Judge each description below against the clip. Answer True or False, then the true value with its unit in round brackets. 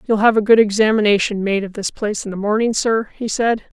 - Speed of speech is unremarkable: False (240 wpm)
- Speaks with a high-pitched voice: True (210 Hz)